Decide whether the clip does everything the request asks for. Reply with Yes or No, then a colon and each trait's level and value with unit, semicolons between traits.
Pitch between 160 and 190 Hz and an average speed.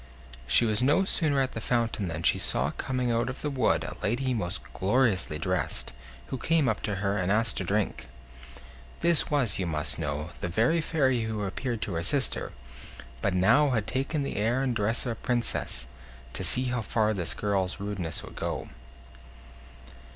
No: low, 110 Hz; average, 185 wpm